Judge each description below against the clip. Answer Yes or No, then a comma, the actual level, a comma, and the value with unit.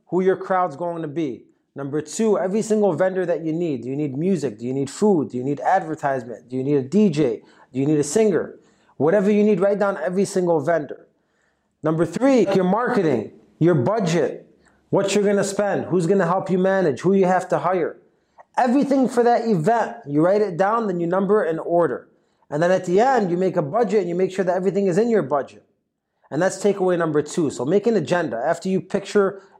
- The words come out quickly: Yes, fast, 225 wpm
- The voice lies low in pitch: No, medium, 185 Hz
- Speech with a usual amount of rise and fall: Yes, average, 3.9 semitones